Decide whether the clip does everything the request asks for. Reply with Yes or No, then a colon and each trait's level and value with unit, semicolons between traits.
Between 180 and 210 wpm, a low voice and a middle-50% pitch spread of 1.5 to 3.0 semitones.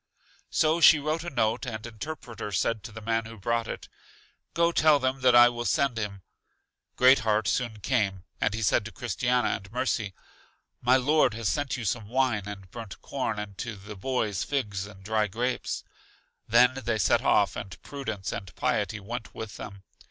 No: average, 185 wpm; low, 115 Hz; average, 3.6 semitones